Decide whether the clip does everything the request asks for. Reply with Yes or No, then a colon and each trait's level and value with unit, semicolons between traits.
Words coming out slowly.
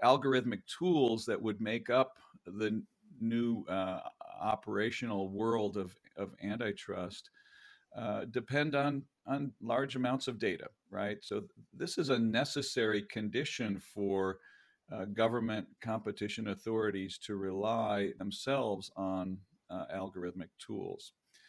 Yes: slow, 115 wpm